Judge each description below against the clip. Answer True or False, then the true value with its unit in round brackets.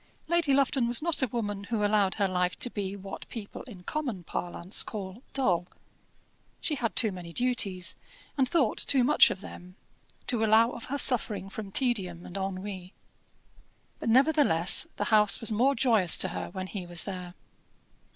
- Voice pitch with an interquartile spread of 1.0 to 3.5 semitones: False (4.8 semitones)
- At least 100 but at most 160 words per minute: False (170 wpm)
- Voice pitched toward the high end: True (210 Hz)